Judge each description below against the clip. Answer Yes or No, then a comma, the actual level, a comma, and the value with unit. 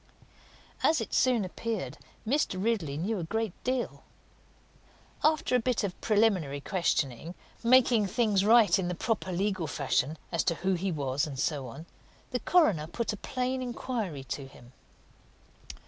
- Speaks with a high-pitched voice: Yes, high, 195 Hz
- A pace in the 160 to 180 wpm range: No, average, 150 wpm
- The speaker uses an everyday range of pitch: No, wide, 6.8 semitones